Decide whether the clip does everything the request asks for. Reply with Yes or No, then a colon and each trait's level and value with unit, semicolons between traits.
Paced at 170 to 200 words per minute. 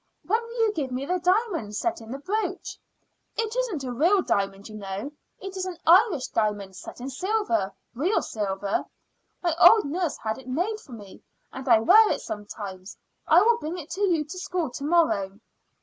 Yes: average, 195 wpm